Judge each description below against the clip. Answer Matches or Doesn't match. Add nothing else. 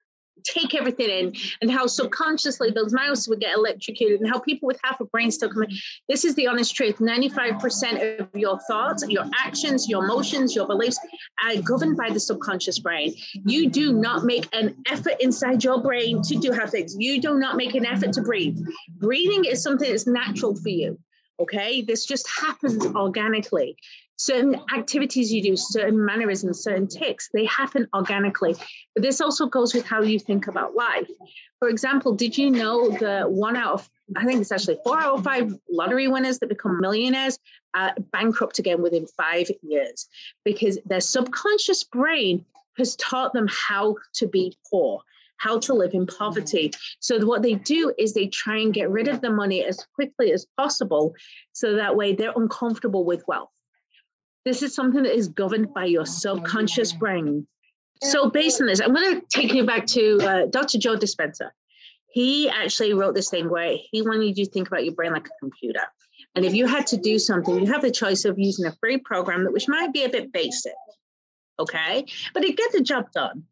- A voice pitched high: Matches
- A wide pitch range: Doesn't match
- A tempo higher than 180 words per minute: Matches